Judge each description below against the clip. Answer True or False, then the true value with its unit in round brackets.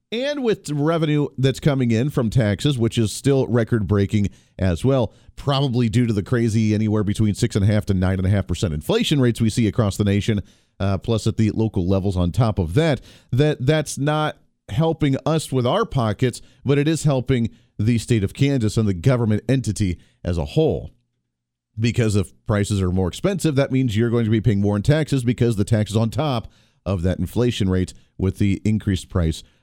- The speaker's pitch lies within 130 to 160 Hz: False (115 Hz)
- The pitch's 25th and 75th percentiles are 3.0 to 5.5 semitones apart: True (4.8 semitones)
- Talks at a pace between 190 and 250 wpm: True (205 wpm)